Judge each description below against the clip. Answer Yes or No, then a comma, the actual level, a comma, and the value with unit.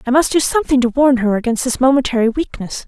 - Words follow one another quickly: Yes, fast, 230 wpm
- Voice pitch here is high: Yes, very high, 255 Hz